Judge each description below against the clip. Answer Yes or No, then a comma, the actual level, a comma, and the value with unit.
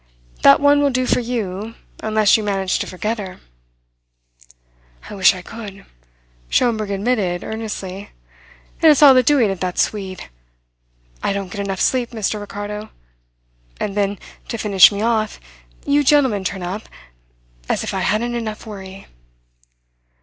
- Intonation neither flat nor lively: Yes, average, 3.1 semitones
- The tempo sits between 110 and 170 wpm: Yes, average, 150 wpm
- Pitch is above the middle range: Yes, high, 210 Hz